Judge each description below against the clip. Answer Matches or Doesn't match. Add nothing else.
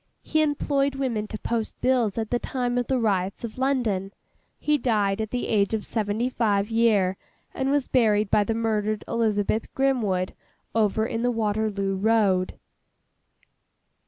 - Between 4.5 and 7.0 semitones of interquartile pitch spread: Doesn't match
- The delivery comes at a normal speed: Matches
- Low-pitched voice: Doesn't match